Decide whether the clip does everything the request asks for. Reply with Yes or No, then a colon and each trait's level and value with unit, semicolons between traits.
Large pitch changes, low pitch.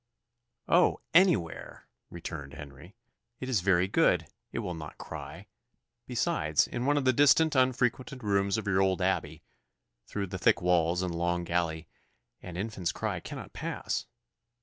Yes: wide, 6.4 semitones; very low, 95 Hz